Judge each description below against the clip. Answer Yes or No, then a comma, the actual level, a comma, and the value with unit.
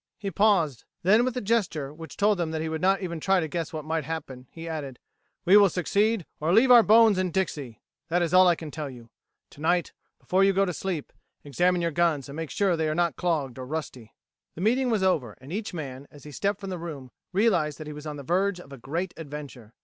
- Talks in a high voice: No, medium, 165 Hz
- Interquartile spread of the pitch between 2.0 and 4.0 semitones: No, average, 4.4 semitones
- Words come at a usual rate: No, fast, 245 wpm